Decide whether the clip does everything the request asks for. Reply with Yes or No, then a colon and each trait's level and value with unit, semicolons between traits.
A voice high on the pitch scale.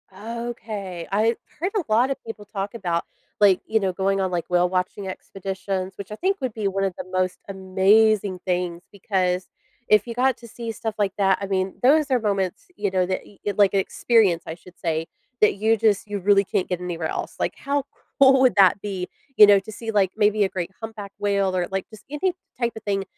Yes: high, 200 Hz